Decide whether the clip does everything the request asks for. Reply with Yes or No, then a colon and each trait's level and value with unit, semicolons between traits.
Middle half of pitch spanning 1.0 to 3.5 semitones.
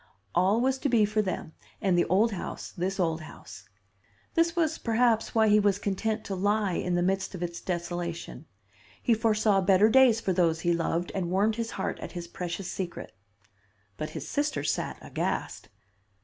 No: average, 4.1 semitones